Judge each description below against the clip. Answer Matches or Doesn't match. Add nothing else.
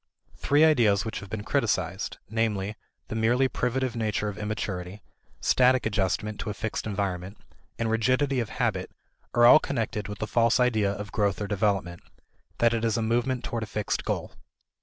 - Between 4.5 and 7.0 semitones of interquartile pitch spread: Doesn't match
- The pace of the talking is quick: Doesn't match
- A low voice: Matches